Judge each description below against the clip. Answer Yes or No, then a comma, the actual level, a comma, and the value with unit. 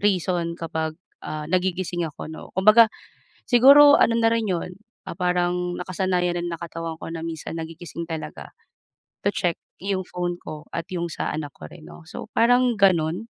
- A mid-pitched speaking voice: Yes, medium, 175 Hz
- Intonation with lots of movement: No, narrow, 2.6 semitones